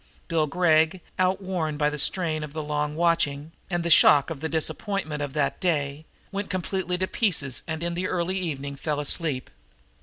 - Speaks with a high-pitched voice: No, medium, 160 Hz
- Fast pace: No, average, 180 wpm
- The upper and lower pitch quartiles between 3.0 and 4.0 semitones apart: Yes, average, 3.4 semitones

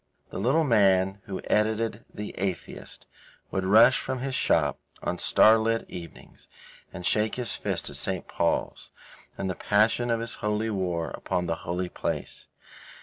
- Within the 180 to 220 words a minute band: No, average, 150 wpm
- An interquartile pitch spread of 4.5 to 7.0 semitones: No, average, 3.4 semitones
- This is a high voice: No, low, 105 Hz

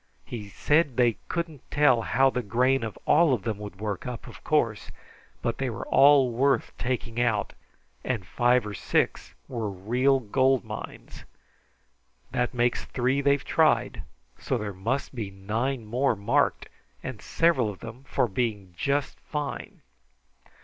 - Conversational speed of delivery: Yes, average, 150 wpm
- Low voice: Yes, low, 120 Hz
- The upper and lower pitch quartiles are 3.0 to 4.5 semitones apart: Yes, average, 3.9 semitones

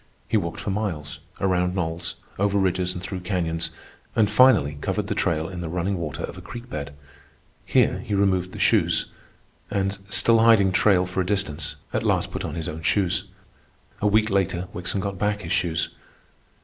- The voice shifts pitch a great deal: No, average, 3.1 semitones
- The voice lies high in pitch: No, very low, 95 Hz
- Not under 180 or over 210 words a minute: Yes, average, 185 wpm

